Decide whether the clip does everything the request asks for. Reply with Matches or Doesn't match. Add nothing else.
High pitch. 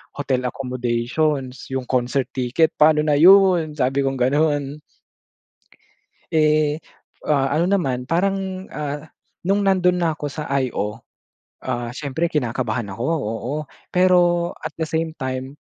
Doesn't match